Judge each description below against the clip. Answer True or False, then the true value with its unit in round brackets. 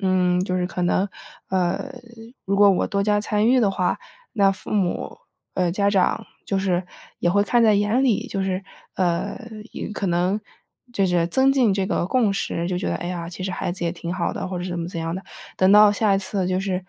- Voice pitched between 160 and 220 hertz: True (190 Hz)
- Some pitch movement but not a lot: False (2.3 semitones)